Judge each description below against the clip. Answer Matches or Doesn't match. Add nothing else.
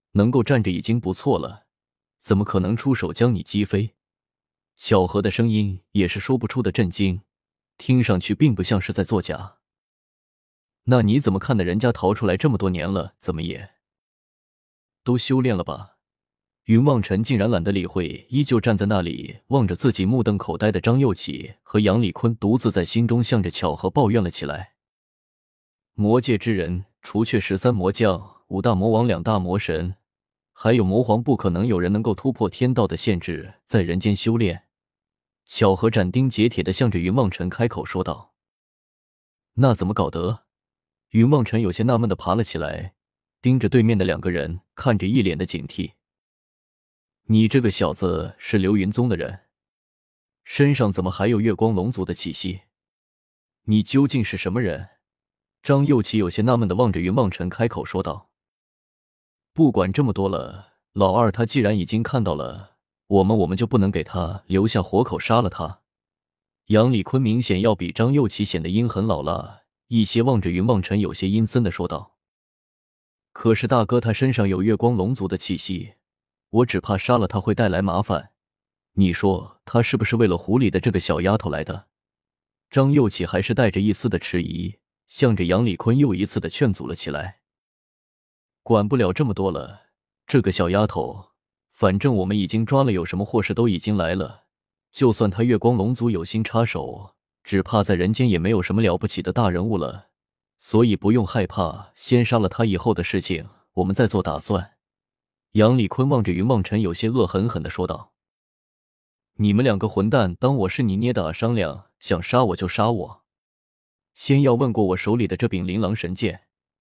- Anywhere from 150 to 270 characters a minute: Matches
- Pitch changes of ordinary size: Matches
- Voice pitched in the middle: Doesn't match